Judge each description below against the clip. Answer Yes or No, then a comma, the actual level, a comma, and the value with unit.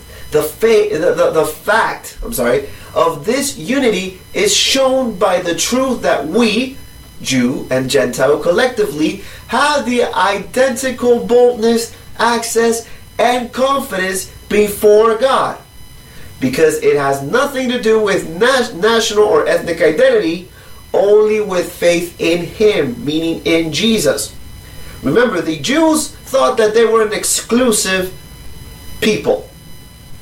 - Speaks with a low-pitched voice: No, high, 225 Hz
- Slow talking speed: Yes, slow, 120 wpm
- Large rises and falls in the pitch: Yes, wide, 6.6 semitones